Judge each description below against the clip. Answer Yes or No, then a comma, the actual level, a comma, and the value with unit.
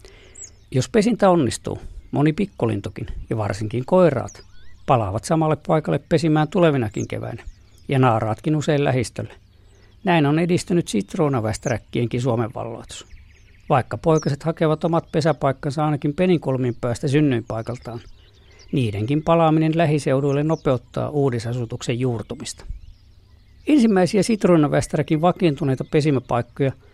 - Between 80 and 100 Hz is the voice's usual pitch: No, low, 130 Hz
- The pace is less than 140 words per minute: Yes, slow, 95 wpm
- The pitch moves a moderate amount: No, wide, 6.4 semitones